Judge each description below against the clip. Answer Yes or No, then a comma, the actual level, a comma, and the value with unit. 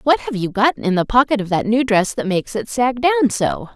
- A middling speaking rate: No, fast, 270 wpm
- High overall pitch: Yes, high, 235 Hz